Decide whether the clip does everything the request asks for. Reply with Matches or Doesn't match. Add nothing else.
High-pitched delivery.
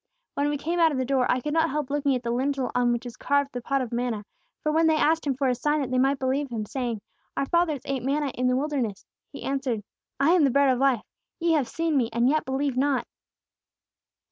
Matches